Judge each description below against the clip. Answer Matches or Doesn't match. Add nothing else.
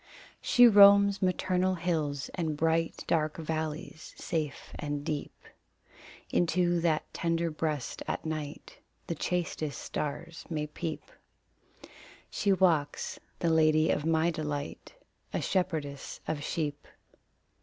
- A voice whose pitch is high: Doesn't match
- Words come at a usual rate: Doesn't match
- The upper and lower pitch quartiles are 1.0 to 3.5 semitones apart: Matches